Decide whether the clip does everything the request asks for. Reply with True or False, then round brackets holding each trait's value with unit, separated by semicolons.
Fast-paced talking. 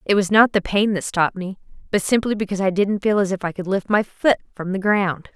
True (270 wpm)